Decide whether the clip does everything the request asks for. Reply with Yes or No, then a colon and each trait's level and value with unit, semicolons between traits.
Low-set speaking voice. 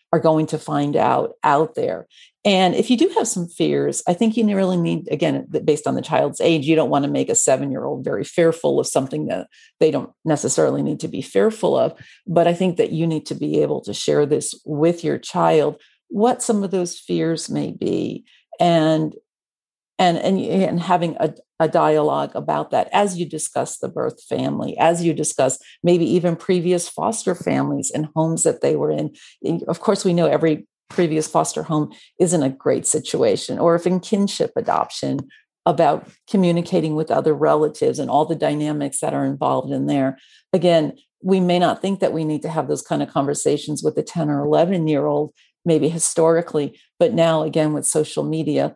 No: medium, 165 Hz